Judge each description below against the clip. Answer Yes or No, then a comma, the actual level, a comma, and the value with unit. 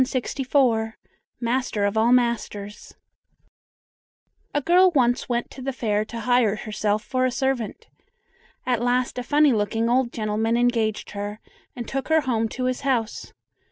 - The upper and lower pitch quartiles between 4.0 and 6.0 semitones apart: No, average, 2.8 semitones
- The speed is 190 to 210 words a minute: No, average, 145 wpm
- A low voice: No, high, 240 Hz